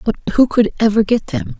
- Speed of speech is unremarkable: No, fast, 225 wpm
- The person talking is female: No, male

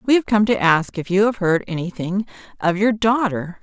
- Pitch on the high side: Yes, high, 200 Hz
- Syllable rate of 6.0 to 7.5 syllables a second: No, 5.0 syllables/s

